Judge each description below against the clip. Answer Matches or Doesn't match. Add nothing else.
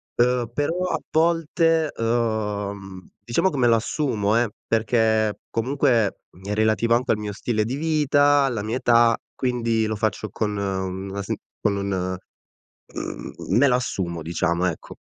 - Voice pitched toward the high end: Doesn't match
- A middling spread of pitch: Matches